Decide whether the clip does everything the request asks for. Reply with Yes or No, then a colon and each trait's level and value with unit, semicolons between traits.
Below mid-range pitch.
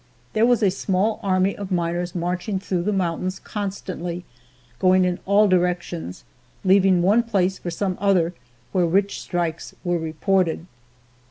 No: medium, 185 Hz